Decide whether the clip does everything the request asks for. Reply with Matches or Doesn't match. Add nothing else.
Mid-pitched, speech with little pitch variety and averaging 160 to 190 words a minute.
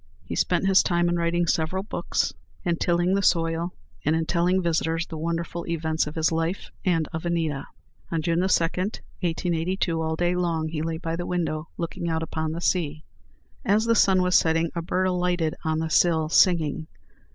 Matches